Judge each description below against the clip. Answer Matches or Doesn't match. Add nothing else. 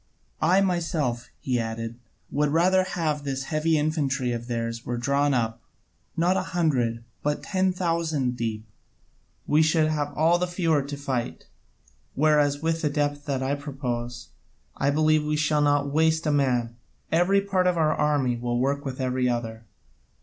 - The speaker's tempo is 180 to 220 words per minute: Doesn't match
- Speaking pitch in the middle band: Matches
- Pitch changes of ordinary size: Matches